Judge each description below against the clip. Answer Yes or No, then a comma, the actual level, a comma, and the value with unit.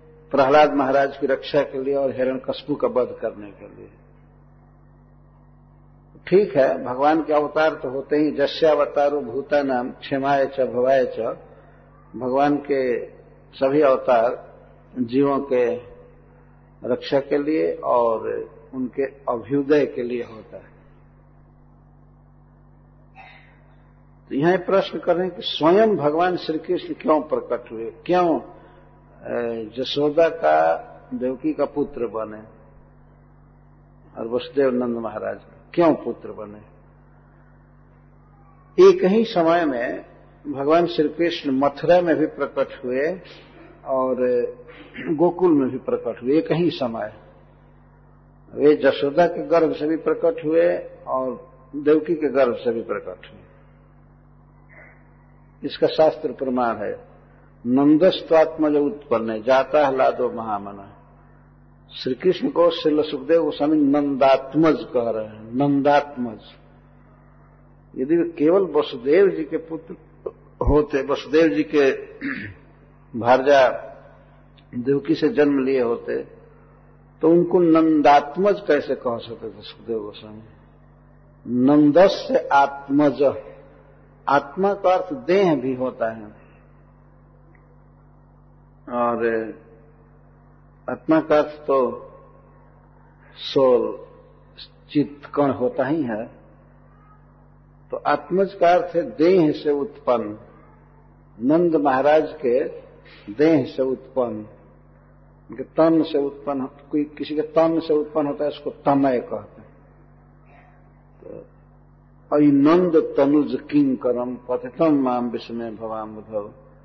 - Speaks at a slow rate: Yes, slow, 105 wpm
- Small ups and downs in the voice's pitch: No, average, 4.2 semitones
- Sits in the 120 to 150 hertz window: Yes, medium, 140 Hz